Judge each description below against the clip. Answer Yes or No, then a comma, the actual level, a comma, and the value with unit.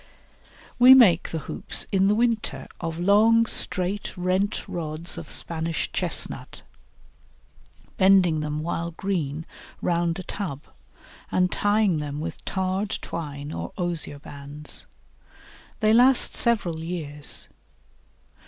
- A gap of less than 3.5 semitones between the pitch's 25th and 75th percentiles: No, average, 4.4 semitones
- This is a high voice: No, medium, 175 Hz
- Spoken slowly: Yes, slow, 115 wpm